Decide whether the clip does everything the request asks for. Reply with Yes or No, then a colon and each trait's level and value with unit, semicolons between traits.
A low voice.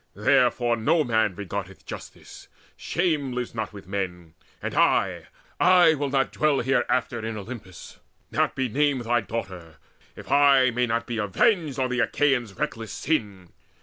Yes: low, 120 Hz